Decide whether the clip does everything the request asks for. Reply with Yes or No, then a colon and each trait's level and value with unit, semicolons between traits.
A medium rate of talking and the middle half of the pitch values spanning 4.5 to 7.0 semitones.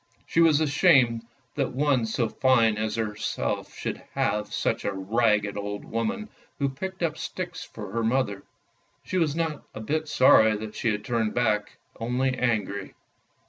Yes: average, 160 wpm; average, 5.2 semitones